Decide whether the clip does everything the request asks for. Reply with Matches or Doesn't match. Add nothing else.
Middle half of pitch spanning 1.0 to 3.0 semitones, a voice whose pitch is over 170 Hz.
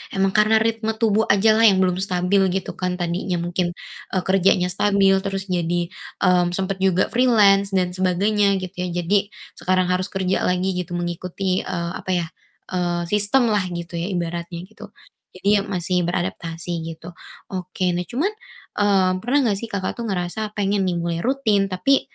Matches